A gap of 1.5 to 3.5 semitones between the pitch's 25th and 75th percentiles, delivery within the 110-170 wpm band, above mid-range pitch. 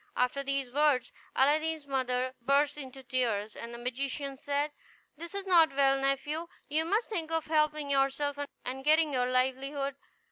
Yes: average, 2.7 semitones; average, 155 wpm; very high, 275 Hz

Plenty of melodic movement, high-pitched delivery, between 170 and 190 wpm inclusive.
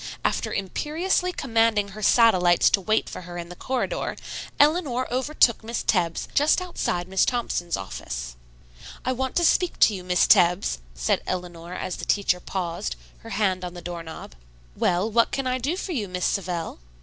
Yes: wide, 6.3 semitones; high, 200 Hz; average, 175 wpm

